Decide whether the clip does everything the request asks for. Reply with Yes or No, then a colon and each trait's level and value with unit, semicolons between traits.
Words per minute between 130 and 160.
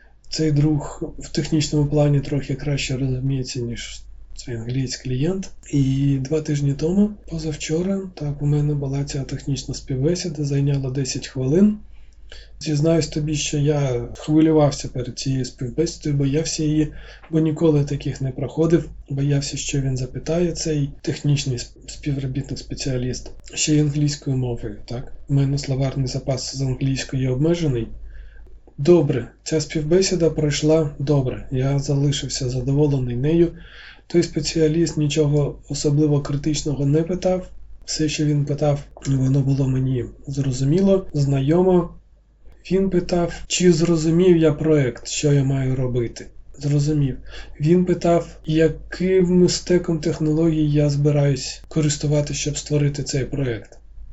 No: average, 120 wpm